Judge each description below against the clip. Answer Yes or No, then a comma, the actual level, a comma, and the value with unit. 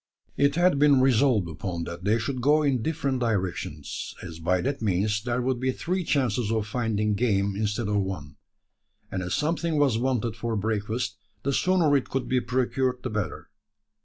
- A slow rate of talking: No, average, 180 wpm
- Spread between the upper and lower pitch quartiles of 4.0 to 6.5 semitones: Yes, average, 4.8 semitones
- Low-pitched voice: Yes, low, 120 Hz